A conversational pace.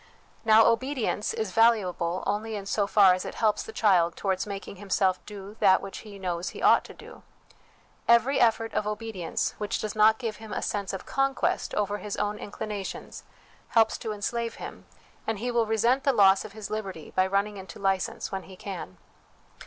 Yes: average, 190 wpm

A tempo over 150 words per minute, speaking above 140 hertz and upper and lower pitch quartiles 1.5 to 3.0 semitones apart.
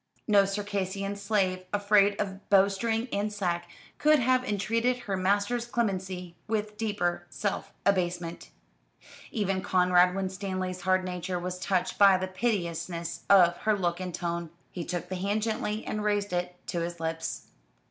No: average, 145 wpm; high, 190 Hz; narrow, 2.5 semitones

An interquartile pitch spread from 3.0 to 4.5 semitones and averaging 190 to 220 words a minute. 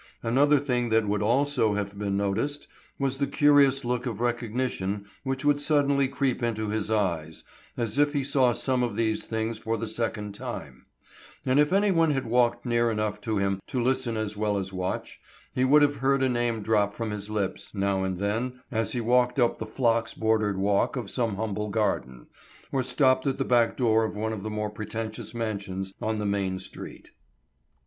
Yes: average, 3.8 semitones; average, 195 wpm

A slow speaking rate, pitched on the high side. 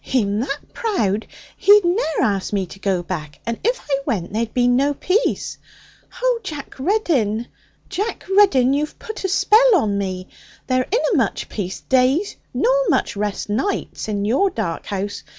No: average, 165 wpm; very high, 255 Hz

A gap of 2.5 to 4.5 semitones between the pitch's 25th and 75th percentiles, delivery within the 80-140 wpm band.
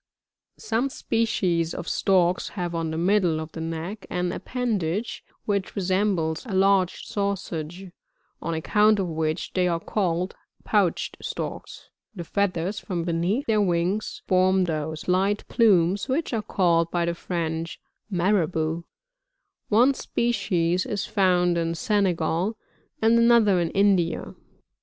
Yes: average, 3.4 semitones; slow, 135 wpm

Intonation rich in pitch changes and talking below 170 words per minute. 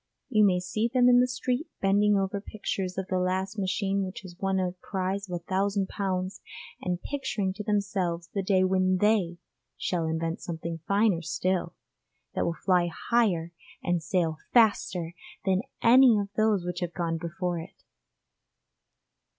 No: narrow, 2.5 semitones; average, 160 wpm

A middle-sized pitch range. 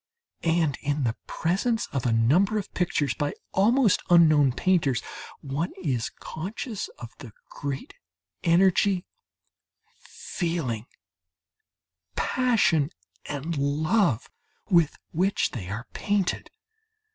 No: wide, 5.8 semitones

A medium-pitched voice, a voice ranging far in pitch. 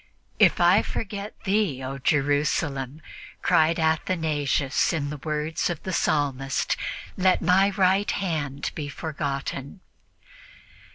No: medium, 155 Hz; average, 4.3 semitones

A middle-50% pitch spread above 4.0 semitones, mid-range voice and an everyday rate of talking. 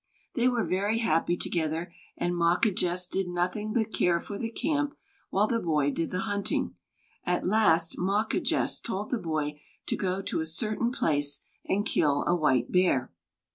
Yes: average, 4.5 semitones; medium, 180 Hz; average, 165 wpm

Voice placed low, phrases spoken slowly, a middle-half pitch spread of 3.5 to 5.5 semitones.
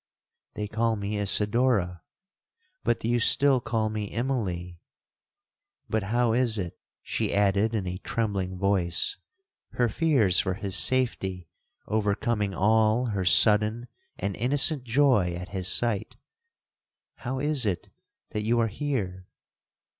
Yes: low, 110 Hz; slow, 125 wpm; average, 3.8 semitones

